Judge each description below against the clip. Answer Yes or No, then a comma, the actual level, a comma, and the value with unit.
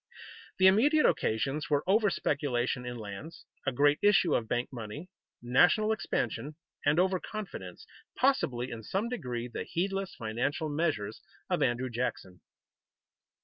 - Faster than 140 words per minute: No, slow, 135 wpm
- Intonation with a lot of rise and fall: Yes, wide, 7.8 semitones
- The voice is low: No, medium, 145 Hz